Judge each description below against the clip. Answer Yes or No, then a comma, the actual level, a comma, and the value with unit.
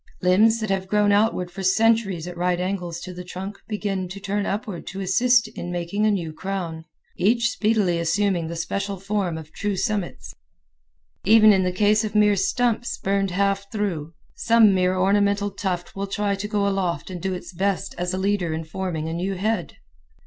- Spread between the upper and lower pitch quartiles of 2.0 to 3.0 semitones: Yes, narrow, 2.6 semitones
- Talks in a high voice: Yes, high, 195 Hz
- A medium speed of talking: Yes, average, 190 wpm